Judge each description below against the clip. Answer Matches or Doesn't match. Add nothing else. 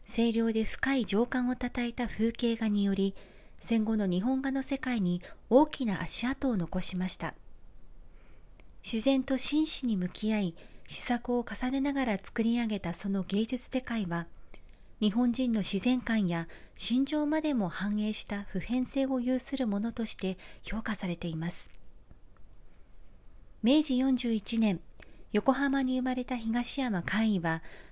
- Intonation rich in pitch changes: Doesn't match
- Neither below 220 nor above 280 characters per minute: Matches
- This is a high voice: Matches